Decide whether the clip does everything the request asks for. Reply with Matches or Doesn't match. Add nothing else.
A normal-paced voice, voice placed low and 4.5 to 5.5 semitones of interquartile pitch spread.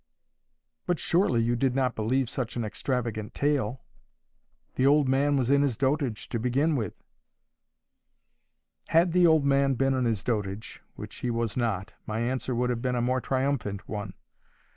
Doesn't match